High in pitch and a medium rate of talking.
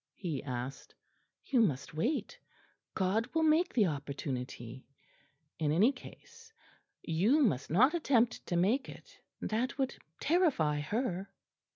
No: high, 200 Hz; slow, 120 wpm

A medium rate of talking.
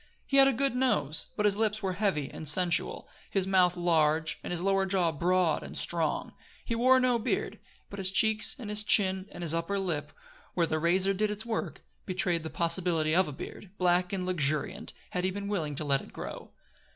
No: fast, 210 wpm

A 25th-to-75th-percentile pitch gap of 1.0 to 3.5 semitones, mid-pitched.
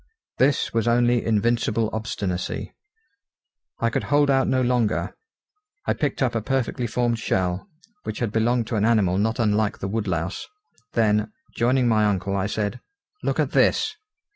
No: average, 2.8 semitones; low, 115 Hz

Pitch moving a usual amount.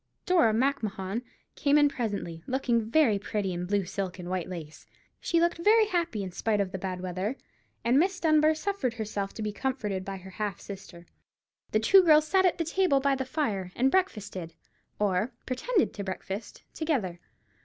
No: wide, 8.0 semitones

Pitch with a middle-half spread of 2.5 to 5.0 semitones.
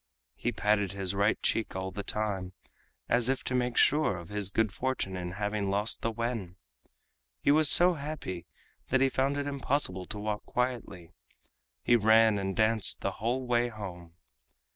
Yes: average, 4.4 semitones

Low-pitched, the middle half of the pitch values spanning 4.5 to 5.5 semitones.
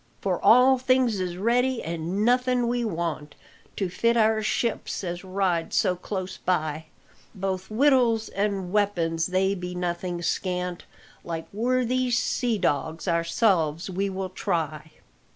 No: high, 190 Hz; average, 4.9 semitones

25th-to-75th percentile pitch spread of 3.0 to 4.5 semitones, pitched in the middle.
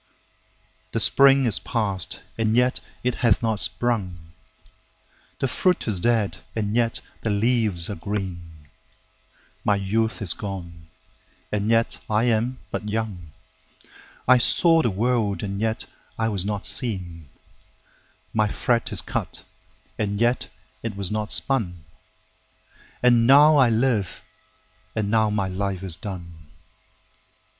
No: average, 3.7 semitones; low, 105 Hz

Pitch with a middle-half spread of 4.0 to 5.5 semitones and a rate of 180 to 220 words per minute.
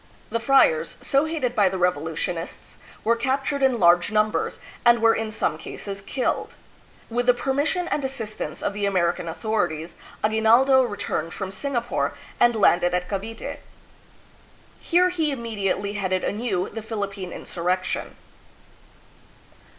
No: average, 5.0 semitones; slow, 135 wpm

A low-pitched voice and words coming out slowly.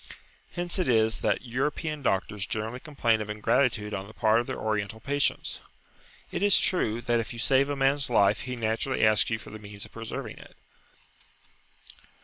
No: low, 115 Hz; average, 180 wpm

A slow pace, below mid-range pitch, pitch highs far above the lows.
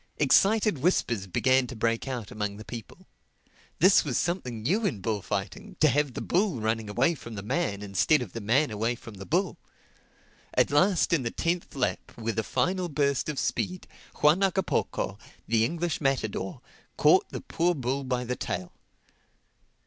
No: average, 170 wpm; low, 125 Hz; wide, 6.7 semitones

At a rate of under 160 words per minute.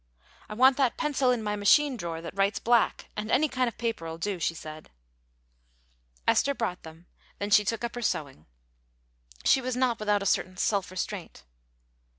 No: average, 175 wpm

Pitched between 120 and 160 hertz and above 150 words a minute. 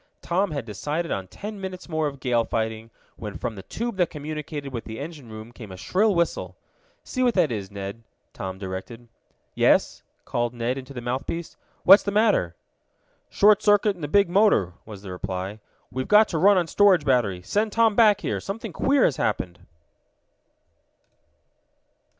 Yes: medium, 140 Hz; average, 175 wpm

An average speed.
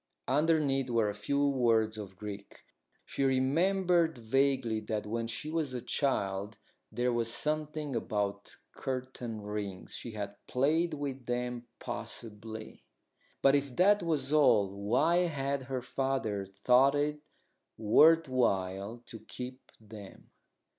No: slow, 125 wpm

